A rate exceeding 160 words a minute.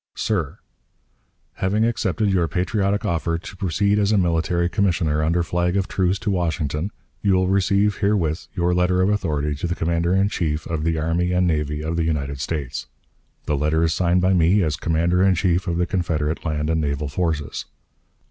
Yes: average, 190 wpm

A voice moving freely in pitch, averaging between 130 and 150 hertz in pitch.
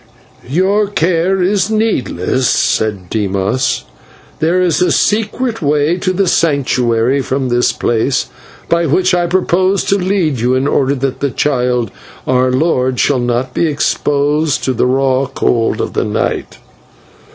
Yes: wide, 6.1 semitones; medium, 140 Hz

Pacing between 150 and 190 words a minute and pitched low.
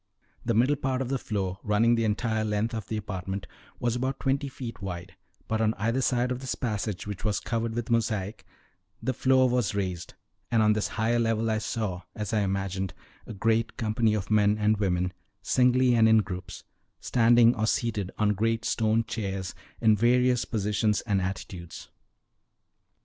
Yes: average, 175 wpm; low, 110 Hz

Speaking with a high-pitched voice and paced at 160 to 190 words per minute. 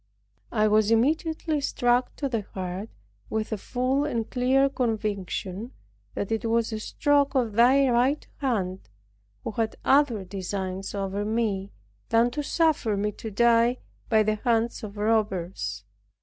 No: high, 225 Hz; average, 145 wpm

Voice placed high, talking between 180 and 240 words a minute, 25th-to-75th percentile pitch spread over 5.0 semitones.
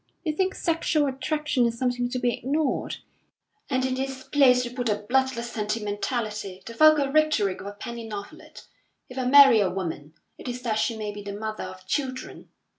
No: high, 245 Hz; average, 190 wpm; average, 4.3 semitones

